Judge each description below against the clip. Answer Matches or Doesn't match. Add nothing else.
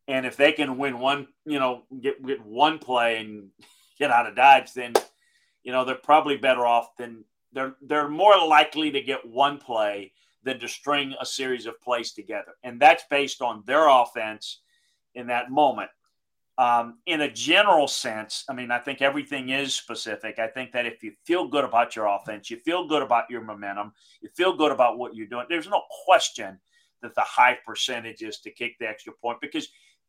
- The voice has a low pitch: Matches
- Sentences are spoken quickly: Doesn't match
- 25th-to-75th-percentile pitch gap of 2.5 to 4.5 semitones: Matches